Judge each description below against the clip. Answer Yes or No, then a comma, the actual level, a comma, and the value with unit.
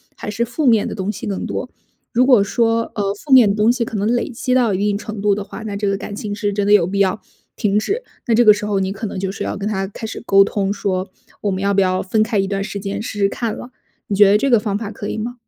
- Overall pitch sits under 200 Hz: No, high, 205 Hz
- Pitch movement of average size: No, narrow, 2.2 semitones